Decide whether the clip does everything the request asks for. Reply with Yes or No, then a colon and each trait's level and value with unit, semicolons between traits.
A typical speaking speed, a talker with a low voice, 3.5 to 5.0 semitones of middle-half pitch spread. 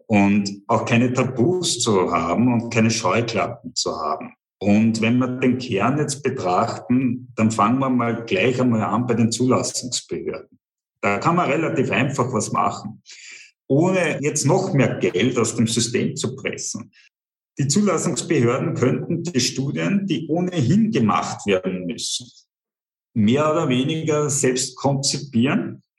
Yes: average, 140 wpm; low, 125 Hz; average, 4.3 semitones